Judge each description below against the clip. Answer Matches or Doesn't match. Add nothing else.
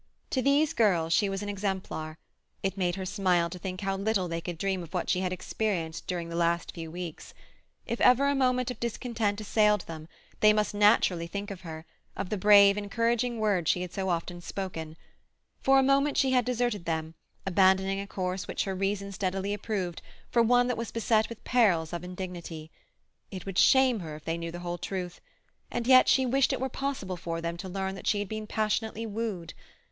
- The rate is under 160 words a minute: Doesn't match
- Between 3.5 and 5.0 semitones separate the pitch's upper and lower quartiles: Matches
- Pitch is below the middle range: Doesn't match